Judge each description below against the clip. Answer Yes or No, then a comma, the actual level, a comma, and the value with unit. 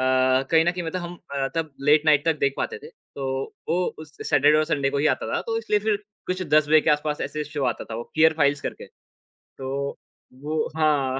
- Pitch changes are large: No, narrow, 2.6 semitones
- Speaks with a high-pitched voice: No, medium, 150 Hz